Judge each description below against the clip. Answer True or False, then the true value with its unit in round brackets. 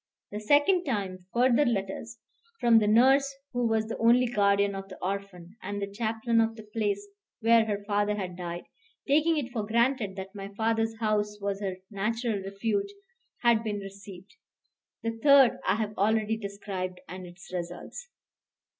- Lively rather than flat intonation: False (2.7 semitones)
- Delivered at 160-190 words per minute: True (165 wpm)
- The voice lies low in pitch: False (215 Hz)